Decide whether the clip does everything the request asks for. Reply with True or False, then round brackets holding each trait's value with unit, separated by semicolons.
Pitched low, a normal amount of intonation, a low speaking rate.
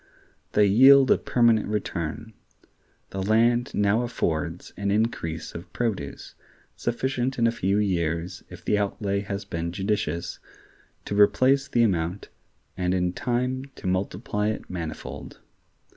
True (100 Hz; 4.6 semitones; 130 wpm)